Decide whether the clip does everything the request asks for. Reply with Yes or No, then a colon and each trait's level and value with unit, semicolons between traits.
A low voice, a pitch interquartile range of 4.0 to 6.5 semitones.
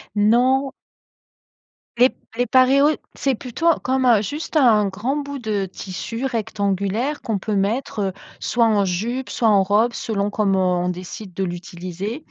No: high, 215 Hz; average, 4.7 semitones